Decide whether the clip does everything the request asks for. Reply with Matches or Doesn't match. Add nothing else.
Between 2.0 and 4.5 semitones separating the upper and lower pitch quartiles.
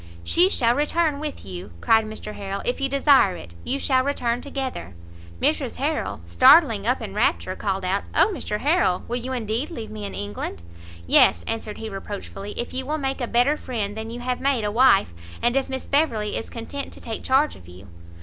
Doesn't match